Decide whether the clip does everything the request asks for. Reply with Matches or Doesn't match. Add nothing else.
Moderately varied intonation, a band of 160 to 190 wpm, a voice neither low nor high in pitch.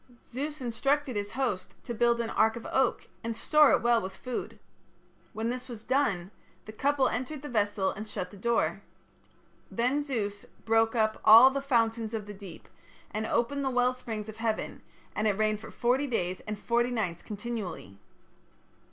Doesn't match